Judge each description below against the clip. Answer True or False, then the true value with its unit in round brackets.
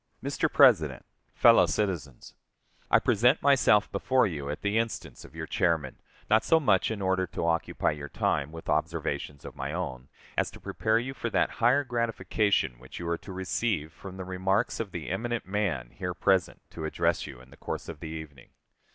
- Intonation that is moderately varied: False (5.9 semitones)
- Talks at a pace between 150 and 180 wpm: False (190 wpm)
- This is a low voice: True (95 Hz)